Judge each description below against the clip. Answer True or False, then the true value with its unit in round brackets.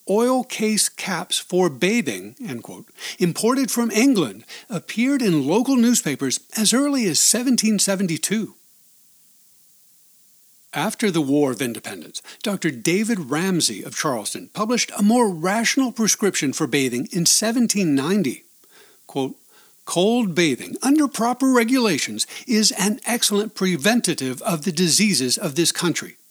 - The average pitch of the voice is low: False (205 Hz)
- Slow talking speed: True (120 wpm)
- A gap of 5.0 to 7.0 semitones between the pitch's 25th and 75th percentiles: True (5.6 semitones)